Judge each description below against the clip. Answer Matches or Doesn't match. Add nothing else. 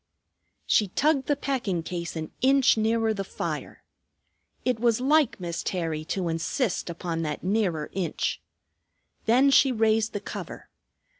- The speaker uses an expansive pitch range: Matches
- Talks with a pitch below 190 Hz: Doesn't match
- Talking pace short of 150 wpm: Matches